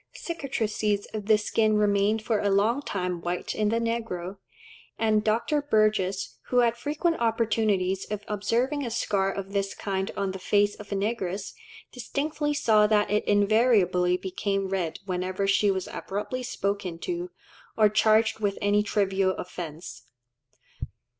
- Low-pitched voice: No, high, 210 Hz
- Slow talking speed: No, average, 145 wpm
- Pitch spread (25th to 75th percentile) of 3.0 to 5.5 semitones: No, narrow, 2.6 semitones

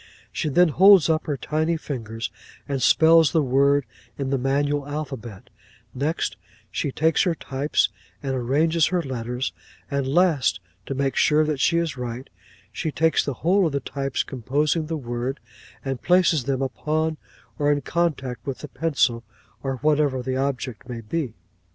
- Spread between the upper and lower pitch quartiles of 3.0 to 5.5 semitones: Yes, average, 3.3 semitones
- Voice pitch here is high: No, medium, 140 Hz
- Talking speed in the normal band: Yes, average, 165 wpm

